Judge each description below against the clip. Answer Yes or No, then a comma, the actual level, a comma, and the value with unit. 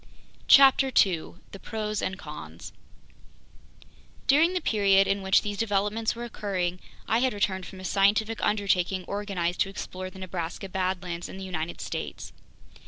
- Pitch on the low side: No, high, 195 Hz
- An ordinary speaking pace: Yes, average, 150 wpm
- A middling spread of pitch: No, narrow, 2.3 semitones